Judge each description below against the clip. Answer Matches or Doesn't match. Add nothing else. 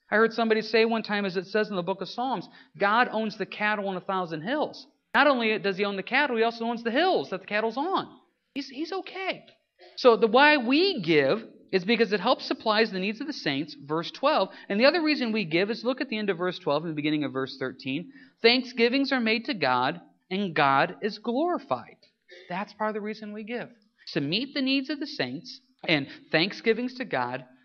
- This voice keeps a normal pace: Doesn't match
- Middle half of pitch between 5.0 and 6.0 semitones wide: Matches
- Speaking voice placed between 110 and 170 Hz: Doesn't match